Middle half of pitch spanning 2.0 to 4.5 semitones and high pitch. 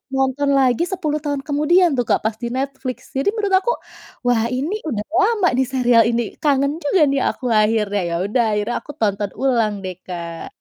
No: average, 4.9 semitones; very high, 260 Hz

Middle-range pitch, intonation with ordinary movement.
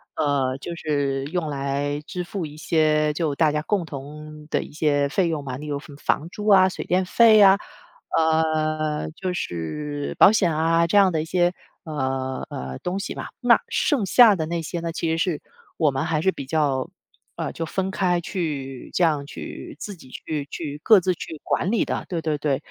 Yes: medium, 155 Hz; average, 3.5 semitones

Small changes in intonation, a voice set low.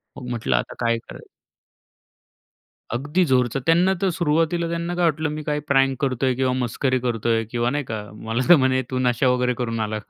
No: average, 4.1 semitones; low, 130 Hz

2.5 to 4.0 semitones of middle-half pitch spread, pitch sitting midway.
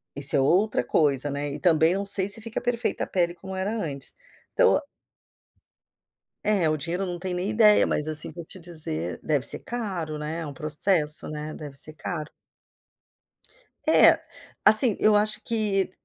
No: average, 5.0 semitones; medium, 175 Hz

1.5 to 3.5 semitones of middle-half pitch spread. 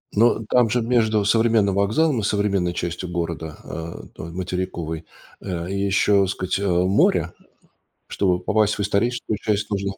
Yes: average, 3.2 semitones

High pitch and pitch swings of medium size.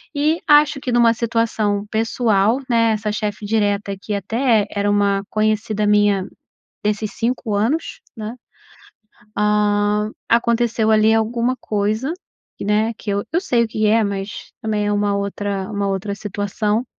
No: high, 215 Hz; narrow, 2.0 semitones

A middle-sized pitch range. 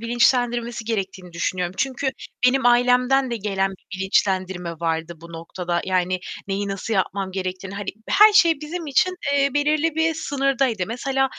No: wide, 6.4 semitones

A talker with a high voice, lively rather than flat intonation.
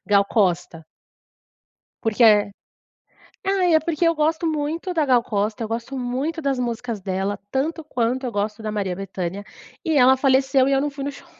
Yes: very high, 250 Hz; wide, 5.7 semitones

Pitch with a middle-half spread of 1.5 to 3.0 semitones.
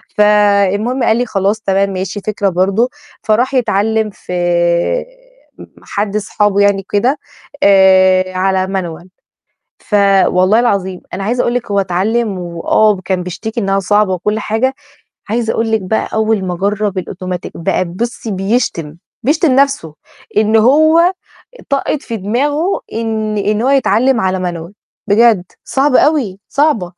No: average, 3.7 semitones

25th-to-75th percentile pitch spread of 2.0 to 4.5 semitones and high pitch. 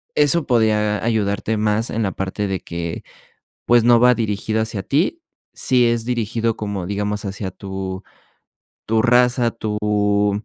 No: narrow, 2.4 semitones; low, 105 Hz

